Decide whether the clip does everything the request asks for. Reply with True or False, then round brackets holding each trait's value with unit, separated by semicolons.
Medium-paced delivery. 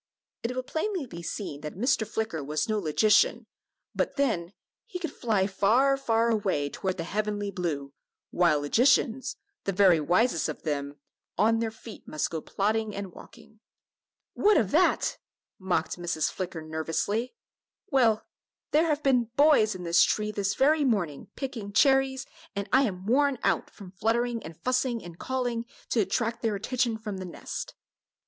True (160 wpm)